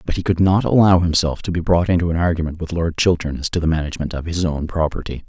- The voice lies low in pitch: Yes, very low, 85 Hz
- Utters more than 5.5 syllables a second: Yes, 6.6 syllables/s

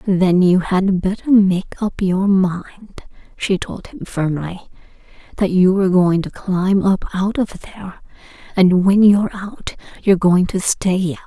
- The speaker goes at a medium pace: Yes, average, 165 wpm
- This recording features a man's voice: No, female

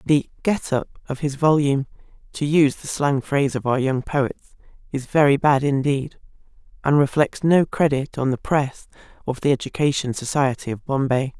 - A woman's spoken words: Yes, female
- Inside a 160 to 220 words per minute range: Yes, average, 170 wpm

